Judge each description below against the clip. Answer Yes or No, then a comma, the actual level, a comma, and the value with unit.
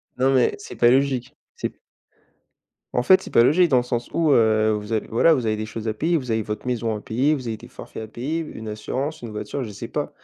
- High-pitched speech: No, low, 120 Hz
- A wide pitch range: No, average, 4.1 semitones